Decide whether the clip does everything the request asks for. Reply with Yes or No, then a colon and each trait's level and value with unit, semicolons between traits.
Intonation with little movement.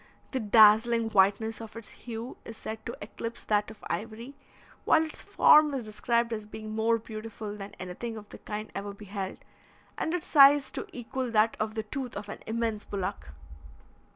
Yes: narrow, 1.9 semitones